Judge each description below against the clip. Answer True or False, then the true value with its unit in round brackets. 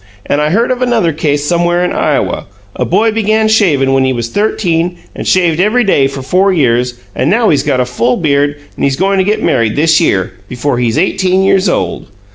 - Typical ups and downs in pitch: False (6.2 semitones)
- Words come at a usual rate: False (215 wpm)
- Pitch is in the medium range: True (170 Hz)